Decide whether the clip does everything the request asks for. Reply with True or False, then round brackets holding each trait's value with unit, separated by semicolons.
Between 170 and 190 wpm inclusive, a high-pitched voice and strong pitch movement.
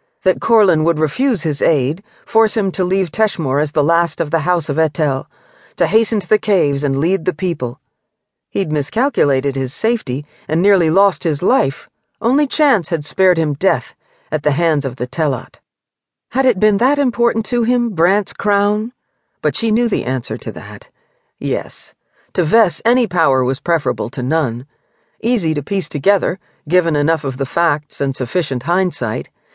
False (175 wpm; 170 Hz; 6.5 semitones)